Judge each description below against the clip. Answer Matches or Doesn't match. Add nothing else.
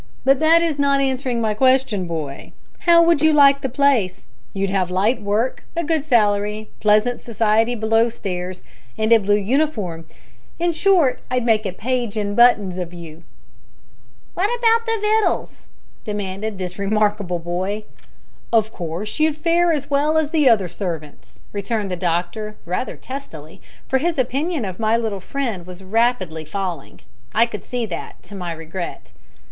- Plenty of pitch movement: Matches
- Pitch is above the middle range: Matches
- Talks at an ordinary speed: Matches